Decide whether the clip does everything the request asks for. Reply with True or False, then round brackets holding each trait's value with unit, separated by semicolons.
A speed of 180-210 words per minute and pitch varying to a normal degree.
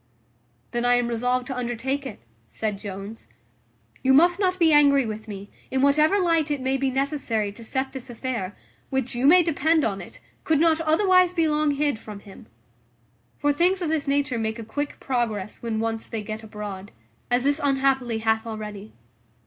True (185 wpm; 4.9 semitones)